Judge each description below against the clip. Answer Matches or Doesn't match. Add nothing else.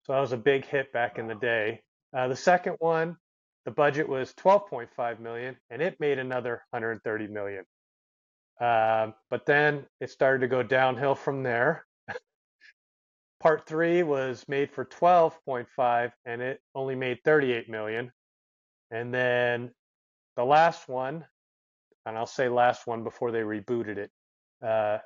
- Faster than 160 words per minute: Doesn't match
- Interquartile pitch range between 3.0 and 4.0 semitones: Matches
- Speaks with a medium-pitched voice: Doesn't match